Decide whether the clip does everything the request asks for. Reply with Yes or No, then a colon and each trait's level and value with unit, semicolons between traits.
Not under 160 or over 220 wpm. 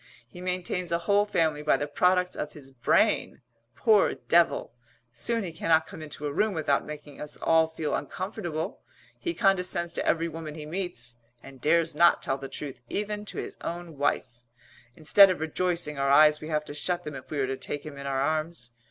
Yes: average, 200 wpm